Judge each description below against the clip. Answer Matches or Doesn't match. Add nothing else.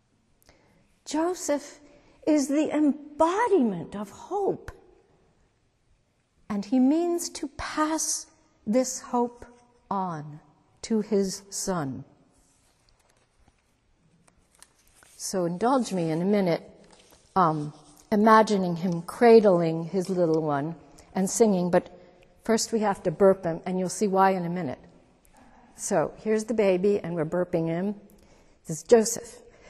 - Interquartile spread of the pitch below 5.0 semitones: Doesn't match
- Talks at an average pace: Doesn't match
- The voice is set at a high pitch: Matches